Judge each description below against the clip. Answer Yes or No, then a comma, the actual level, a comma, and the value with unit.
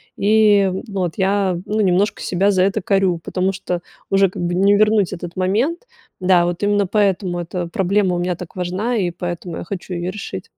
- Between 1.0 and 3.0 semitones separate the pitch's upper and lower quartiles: Yes, narrow, 2.4 semitones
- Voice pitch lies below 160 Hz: No, high, 190 Hz